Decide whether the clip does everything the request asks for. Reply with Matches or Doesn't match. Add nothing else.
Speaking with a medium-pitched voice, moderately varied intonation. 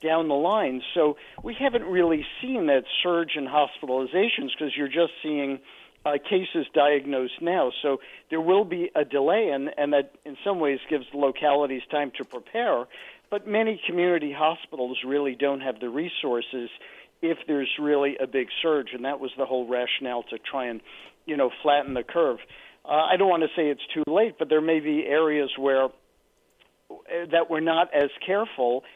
Matches